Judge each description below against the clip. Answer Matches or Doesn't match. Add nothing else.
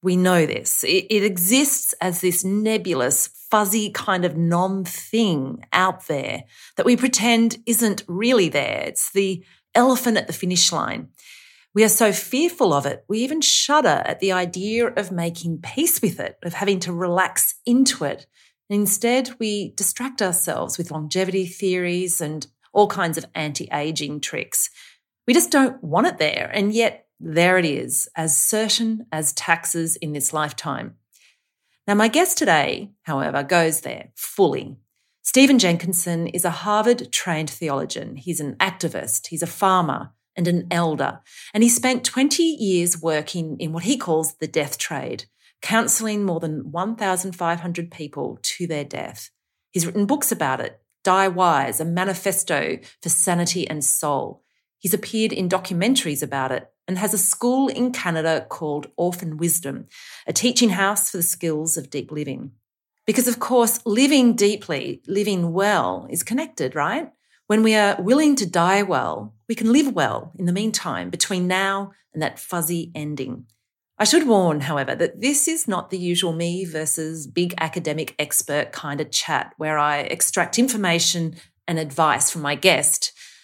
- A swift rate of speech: Doesn't match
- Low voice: Doesn't match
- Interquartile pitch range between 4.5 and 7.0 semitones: Matches